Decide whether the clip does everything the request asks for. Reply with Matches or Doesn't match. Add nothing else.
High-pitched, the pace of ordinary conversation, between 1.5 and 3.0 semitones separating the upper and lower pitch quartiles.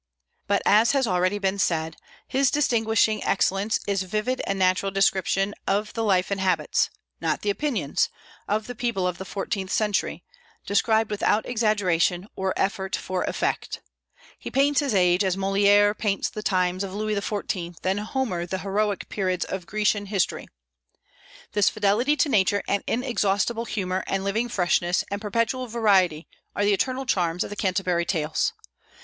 Matches